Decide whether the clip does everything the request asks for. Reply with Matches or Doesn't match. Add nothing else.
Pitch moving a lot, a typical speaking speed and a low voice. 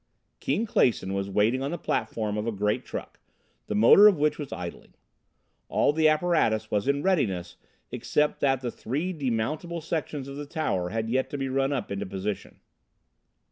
Matches